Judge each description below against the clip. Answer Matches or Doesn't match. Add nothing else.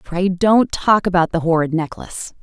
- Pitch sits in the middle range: Matches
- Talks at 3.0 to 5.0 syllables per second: Matches